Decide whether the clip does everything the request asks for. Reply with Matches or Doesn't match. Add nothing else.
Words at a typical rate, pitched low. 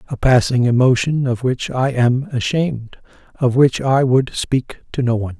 Matches